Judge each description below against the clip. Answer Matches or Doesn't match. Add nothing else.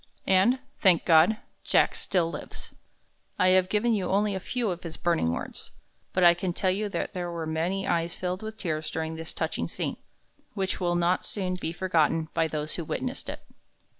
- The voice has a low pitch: Doesn't match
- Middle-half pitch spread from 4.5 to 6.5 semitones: Doesn't match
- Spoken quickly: Doesn't match